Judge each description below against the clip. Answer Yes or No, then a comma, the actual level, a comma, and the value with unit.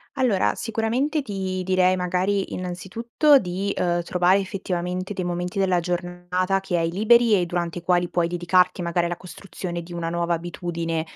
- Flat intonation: Yes, narrow, 1.9 semitones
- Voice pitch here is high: No, medium, 180 Hz